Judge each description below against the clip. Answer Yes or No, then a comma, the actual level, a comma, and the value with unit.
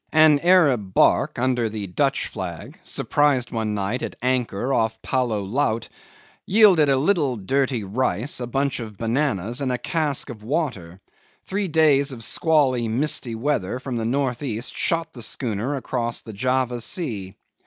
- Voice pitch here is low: Yes, low, 125 Hz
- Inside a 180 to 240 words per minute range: No, average, 155 wpm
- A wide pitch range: No, average, 4.4 semitones